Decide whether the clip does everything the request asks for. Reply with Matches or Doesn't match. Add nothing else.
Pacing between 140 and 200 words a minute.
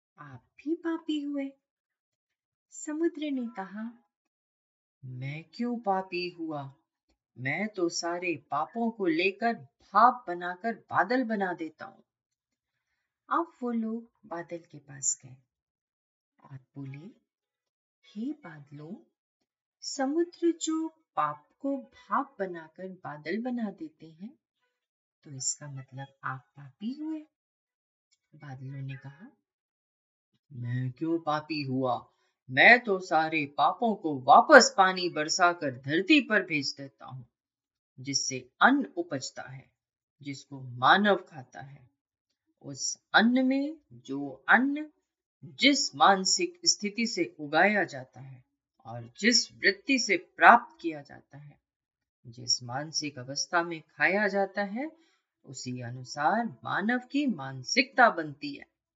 Doesn't match